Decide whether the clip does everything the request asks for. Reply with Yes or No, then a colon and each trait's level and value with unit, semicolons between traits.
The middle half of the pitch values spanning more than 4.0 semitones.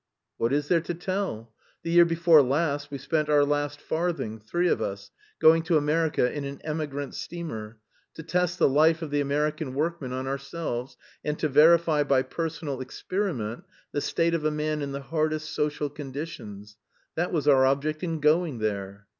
No: average, 3.2 semitones